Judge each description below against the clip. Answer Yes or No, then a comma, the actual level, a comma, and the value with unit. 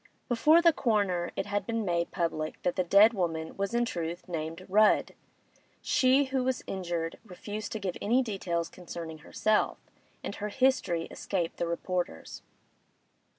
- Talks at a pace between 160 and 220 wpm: No, average, 150 wpm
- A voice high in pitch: Yes, high, 195 Hz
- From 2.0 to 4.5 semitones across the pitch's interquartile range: No, average, 4.9 semitones